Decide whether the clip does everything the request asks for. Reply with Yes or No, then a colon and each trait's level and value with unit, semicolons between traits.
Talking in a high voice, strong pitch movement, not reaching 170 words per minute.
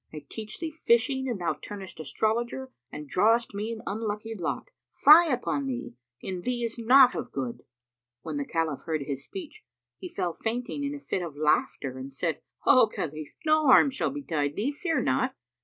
No: high, 220 Hz; wide, 9.0 semitones; average, 185 wpm